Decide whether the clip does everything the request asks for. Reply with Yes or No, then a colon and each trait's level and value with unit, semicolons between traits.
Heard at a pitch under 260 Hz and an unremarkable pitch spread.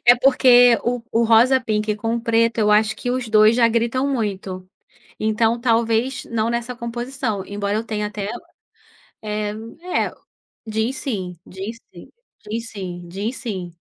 No: high, 225 Hz; narrow, 2.2 semitones